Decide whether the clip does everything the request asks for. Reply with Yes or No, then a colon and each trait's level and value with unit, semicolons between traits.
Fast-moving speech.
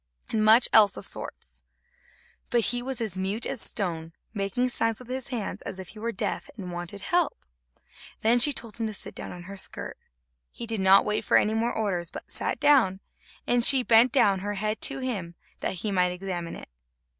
Yes: fast, 215 wpm